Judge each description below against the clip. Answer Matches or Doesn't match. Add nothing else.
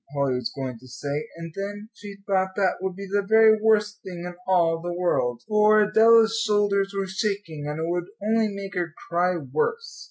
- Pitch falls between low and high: Doesn't match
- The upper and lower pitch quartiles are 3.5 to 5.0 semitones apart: Matches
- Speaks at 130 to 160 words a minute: Doesn't match